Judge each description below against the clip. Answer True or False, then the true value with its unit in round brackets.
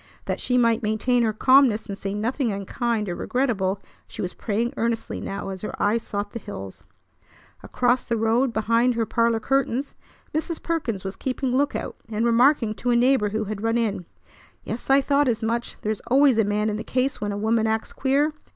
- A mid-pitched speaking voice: False (230 Hz)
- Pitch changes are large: False (3.1 semitones)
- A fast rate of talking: False (195 wpm)